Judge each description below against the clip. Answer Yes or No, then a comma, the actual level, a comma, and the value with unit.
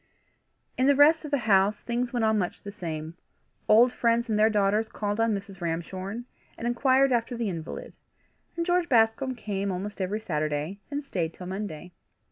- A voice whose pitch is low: No, high, 215 Hz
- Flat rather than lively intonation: No, average, 4.2 semitones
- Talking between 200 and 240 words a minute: No, average, 180 wpm